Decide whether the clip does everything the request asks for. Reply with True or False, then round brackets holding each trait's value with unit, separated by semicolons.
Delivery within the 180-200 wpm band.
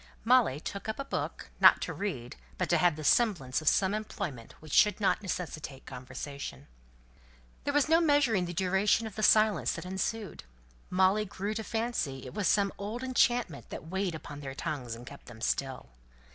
True (185 wpm)